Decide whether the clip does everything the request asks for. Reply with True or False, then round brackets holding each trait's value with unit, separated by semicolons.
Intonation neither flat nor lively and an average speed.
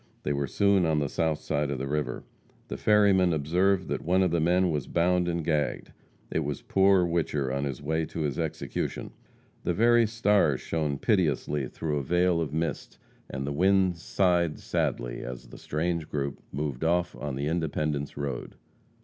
True (3.9 semitones; 180 wpm)